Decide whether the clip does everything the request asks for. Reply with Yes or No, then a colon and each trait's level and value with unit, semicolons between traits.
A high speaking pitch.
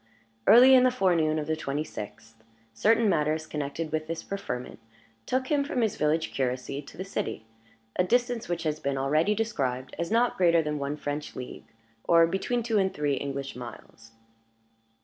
No: medium, 155 Hz